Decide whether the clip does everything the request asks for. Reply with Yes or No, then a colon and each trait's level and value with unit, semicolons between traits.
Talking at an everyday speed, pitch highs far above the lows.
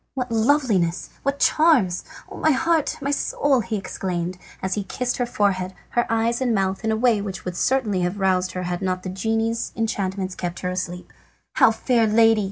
No: average, 190 wpm; average, 4.6 semitones